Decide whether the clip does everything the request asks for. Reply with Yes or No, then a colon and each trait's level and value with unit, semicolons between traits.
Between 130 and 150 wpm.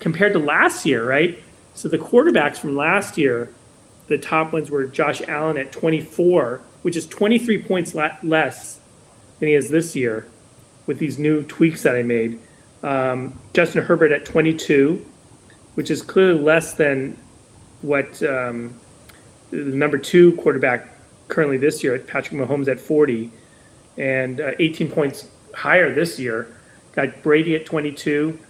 Yes: average, 145 wpm